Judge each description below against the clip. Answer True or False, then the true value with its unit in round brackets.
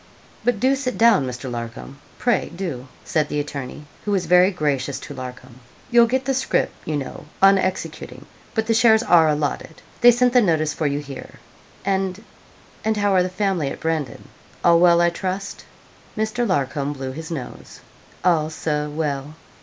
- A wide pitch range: True (6.0 semitones)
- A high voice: False (165 Hz)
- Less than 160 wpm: False (175 wpm)